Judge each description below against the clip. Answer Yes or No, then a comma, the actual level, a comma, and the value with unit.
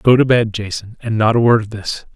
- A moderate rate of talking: No, fast, 250 wpm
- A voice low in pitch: Yes, low, 110 Hz